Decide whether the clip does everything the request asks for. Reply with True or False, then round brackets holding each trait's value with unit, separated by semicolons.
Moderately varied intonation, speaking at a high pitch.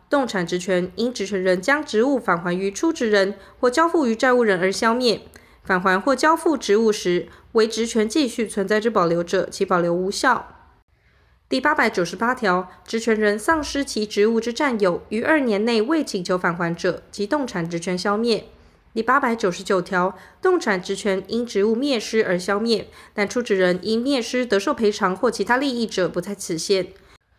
True (4.3 semitones; 210 Hz)